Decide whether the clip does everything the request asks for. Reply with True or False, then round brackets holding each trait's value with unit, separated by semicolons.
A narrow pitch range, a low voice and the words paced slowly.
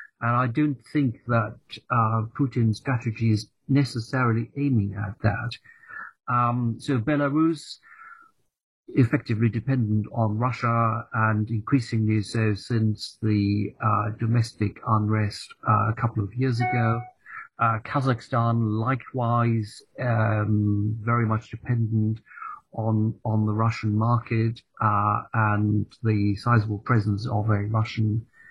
True (2.2 semitones; 115 Hz; 115 wpm)